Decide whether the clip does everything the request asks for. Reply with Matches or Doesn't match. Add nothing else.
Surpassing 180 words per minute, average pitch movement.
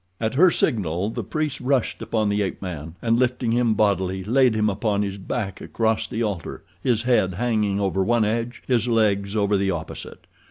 Matches